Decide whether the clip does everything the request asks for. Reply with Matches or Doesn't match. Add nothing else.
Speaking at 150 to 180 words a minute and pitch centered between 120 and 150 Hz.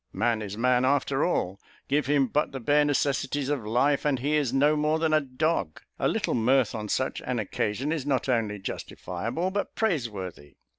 Doesn't match